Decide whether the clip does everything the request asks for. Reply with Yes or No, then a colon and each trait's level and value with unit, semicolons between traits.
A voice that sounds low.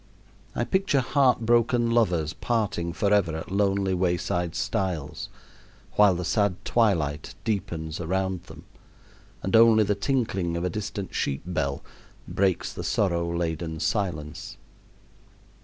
Yes: very low, 95 Hz